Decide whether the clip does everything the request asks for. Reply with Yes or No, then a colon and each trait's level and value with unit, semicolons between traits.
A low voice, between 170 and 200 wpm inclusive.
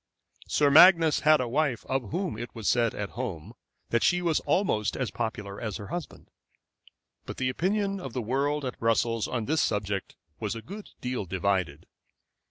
Yes: low, 125 Hz; average, 175 wpm